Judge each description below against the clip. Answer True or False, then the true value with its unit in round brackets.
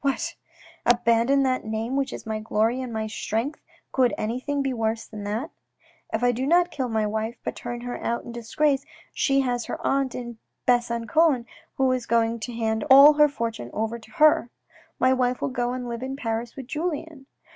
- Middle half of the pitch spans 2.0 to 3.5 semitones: True (2.9 semitones)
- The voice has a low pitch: False (245 Hz)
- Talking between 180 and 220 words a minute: True (200 wpm)